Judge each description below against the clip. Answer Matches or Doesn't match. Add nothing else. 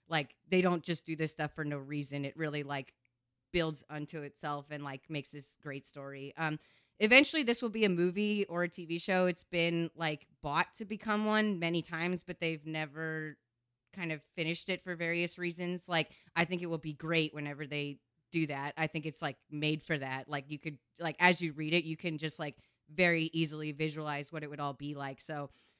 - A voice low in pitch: Doesn't match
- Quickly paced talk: Matches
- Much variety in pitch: Doesn't match